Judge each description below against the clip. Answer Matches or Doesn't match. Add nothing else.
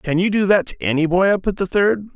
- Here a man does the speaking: Matches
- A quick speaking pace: Matches